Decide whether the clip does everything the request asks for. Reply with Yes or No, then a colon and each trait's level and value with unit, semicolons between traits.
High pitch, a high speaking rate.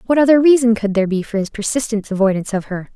Yes: high, 220 Hz; fast, 245 wpm